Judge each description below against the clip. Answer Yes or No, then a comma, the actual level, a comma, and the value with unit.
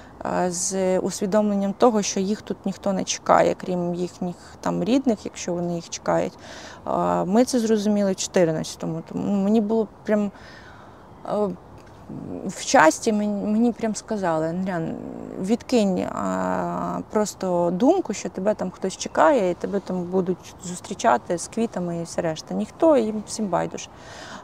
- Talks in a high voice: Yes, high, 195 Hz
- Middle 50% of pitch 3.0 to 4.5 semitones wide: Yes, average, 3.4 semitones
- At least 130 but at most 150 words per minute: Yes, average, 140 wpm